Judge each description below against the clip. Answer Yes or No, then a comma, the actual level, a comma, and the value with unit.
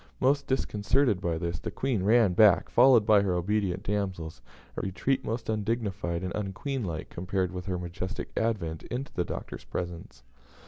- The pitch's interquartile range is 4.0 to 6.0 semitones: Yes, average, 4.3 semitones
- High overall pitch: No, low, 100 Hz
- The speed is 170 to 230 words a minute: No, average, 155 wpm